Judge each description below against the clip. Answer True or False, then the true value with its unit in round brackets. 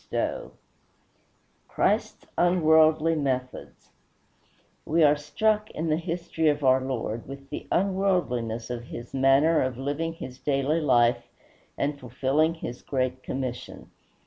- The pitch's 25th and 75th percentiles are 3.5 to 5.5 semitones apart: True (4.1 semitones)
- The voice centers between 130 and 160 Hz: True (140 Hz)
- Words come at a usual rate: False (120 wpm)